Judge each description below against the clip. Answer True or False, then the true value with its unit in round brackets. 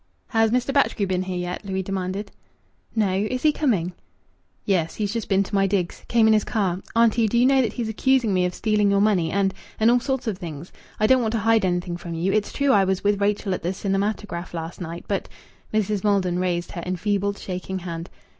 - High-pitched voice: True (200 Hz)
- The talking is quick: True (225 wpm)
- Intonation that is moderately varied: True (3.2 semitones)